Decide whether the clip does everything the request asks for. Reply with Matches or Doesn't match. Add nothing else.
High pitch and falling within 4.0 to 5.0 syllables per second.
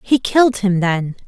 Matches